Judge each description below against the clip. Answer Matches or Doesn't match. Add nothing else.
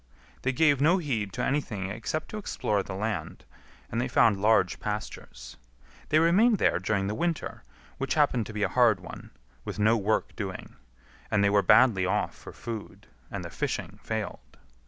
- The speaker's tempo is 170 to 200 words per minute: Matches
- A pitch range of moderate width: Doesn't match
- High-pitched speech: Doesn't match